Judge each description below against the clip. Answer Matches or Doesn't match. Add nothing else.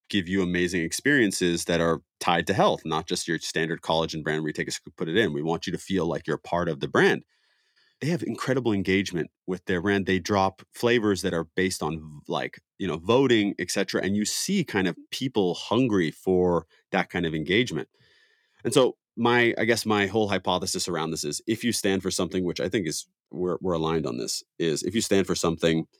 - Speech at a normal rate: Doesn't match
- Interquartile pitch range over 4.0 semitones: Doesn't match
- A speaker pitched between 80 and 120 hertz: Matches